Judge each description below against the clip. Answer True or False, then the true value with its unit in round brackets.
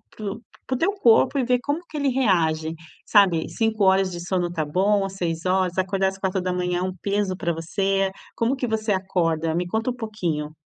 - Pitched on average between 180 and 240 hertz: True (190 Hz)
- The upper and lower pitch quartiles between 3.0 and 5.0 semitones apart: True (3.9 semitones)